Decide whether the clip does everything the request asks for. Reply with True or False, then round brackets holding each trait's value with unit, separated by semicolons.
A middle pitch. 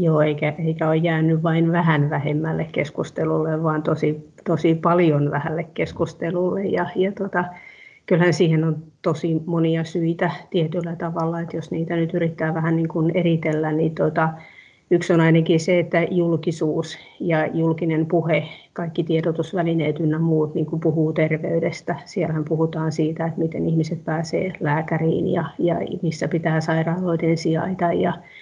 True (165 Hz)